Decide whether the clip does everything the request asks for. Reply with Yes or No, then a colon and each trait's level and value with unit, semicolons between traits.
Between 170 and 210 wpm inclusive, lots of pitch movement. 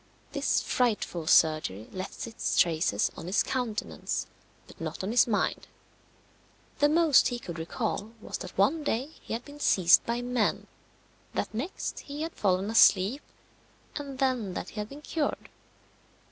No: average, 155 wpm; wide, 6.5 semitones